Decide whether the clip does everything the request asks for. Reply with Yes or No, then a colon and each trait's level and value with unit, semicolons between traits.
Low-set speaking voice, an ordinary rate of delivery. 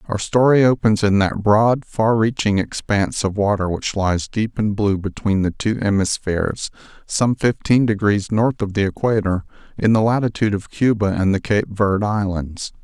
Yes: low, 105 Hz; average, 175 wpm